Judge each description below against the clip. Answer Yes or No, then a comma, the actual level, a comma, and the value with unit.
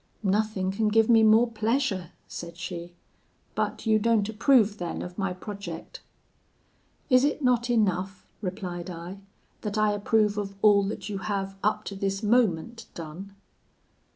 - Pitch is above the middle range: Yes, high, 205 Hz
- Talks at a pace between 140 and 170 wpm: Yes, average, 150 wpm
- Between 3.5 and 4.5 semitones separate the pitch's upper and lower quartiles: No, average, 2.8 semitones